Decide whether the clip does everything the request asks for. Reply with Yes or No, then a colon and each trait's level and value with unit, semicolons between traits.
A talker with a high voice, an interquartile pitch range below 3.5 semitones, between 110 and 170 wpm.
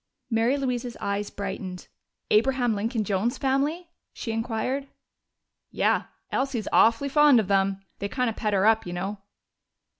No: high, 225 Hz; average, 4.5 semitones; average, 145 wpm